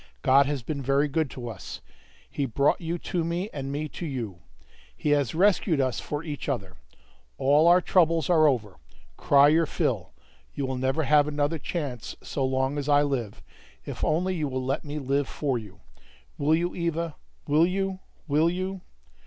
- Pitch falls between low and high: Yes, medium, 145 Hz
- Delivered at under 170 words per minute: No, average, 180 wpm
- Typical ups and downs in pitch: Yes, average, 3.6 semitones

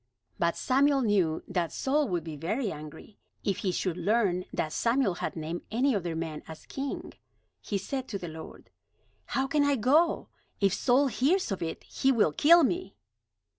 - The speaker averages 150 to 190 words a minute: Yes, average, 175 wpm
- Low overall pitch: No, high, 205 Hz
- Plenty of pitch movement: Yes, wide, 7.9 semitones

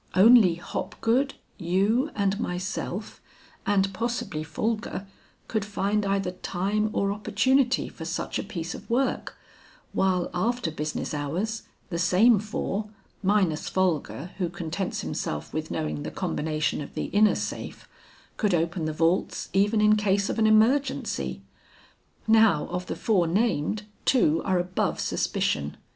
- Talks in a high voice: Yes, high, 195 Hz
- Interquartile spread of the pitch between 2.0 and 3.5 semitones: No, average, 4.2 semitones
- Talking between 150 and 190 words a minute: No, slow, 135 wpm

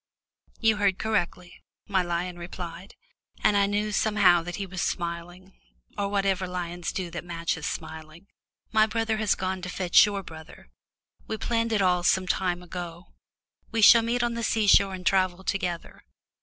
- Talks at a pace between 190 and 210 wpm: No, average, 170 wpm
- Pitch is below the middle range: No, medium, 185 Hz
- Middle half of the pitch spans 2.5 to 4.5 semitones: Yes, average, 2.8 semitones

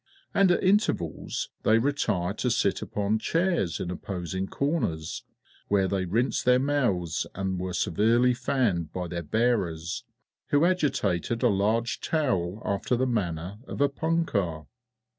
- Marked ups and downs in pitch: Yes, wide, 6.5 semitones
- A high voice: No, low, 105 Hz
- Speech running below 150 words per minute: Yes, average, 140 wpm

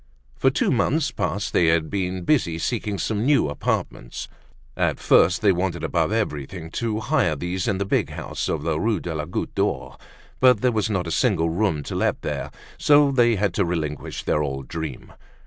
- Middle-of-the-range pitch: No, very low, 90 Hz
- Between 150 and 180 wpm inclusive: No, average, 200 wpm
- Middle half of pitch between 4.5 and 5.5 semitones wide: Yes, average, 5.2 semitones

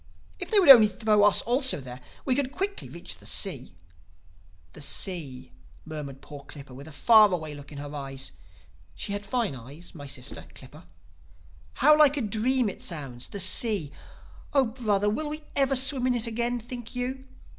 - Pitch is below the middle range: No, high, 210 Hz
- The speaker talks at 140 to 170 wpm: No, average, 180 wpm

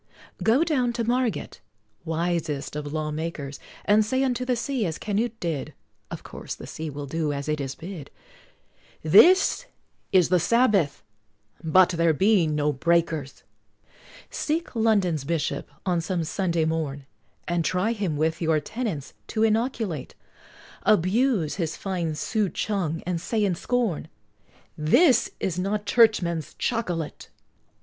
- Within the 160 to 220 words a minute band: No, slow, 135 wpm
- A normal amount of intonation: No, wide, 5.9 semitones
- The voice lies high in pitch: No, medium, 175 Hz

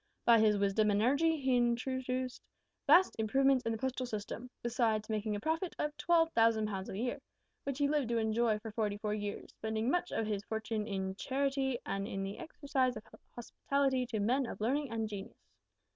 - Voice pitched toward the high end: Yes, high, 235 Hz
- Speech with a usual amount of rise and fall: Yes, average, 3.9 semitones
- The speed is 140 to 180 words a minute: No, average, 190 wpm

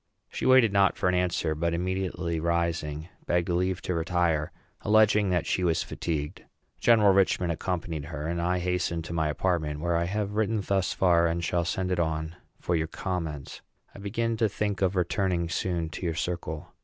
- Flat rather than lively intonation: Yes, narrow, 2.3 semitones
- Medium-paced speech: Yes, average, 185 wpm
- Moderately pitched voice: No, very low, 85 Hz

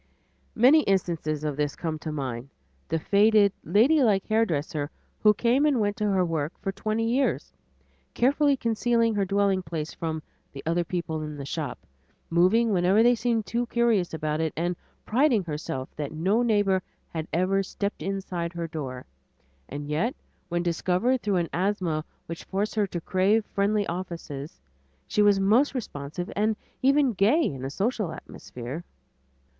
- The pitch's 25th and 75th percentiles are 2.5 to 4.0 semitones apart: No, wide, 5.4 semitones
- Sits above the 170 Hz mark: Yes, high, 190 Hz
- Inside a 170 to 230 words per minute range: No, average, 160 wpm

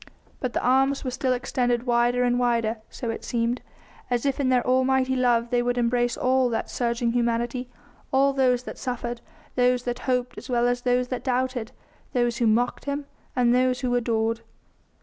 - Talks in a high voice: Yes, high, 245 Hz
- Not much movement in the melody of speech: Yes, narrow, 1.1 semitones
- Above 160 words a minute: Yes, average, 185 wpm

